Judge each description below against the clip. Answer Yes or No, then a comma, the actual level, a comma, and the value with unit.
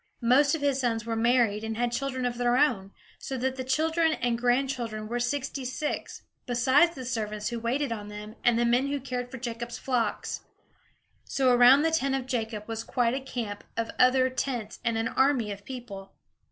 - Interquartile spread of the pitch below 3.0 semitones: Yes, narrow, 2.6 semitones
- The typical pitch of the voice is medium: No, high, 245 Hz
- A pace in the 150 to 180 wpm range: No, average, 195 wpm